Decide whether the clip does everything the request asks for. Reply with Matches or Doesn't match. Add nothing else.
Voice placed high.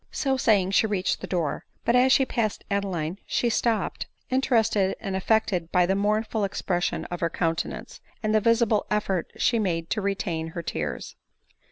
Matches